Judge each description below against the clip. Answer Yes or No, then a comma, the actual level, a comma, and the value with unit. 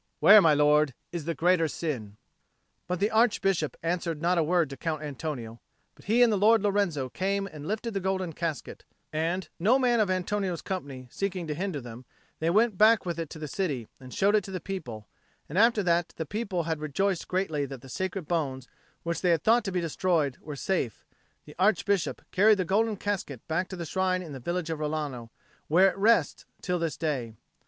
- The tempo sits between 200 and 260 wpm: Yes, fast, 205 wpm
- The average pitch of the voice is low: No, medium, 175 Hz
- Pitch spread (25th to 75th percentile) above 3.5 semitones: Yes, average, 4.5 semitones